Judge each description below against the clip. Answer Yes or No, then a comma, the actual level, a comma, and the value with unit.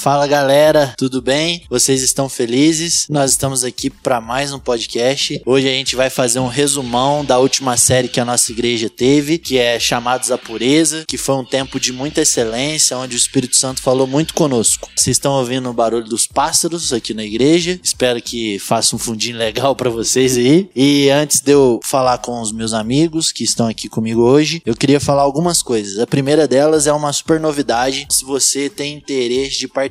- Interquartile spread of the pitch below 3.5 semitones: Yes, average, 2.8 semitones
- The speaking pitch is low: Yes, low, 130 Hz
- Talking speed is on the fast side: Yes, fast, 200 wpm